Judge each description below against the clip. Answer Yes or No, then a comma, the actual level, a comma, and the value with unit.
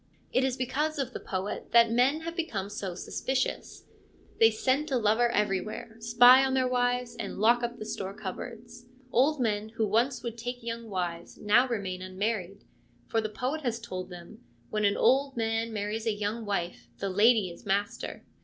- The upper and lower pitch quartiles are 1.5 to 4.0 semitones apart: Yes, average, 3.4 semitones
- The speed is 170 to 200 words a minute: Yes, average, 185 wpm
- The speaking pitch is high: Yes, high, 225 Hz